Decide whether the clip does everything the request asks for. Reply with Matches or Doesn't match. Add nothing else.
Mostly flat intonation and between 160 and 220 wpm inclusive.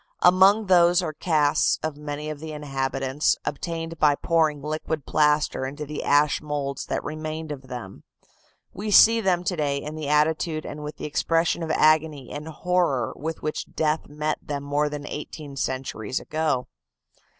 Matches